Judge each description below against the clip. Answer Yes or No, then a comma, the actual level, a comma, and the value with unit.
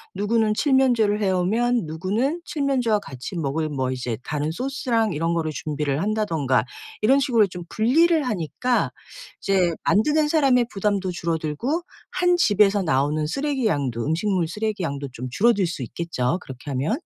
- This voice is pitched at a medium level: No, high, 195 Hz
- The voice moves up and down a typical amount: No, wide, 7.7 semitones